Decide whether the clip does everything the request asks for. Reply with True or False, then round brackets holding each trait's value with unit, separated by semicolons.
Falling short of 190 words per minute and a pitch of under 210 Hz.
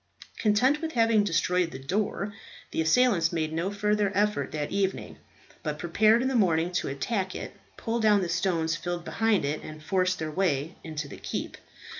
True (180 wpm; 185 Hz)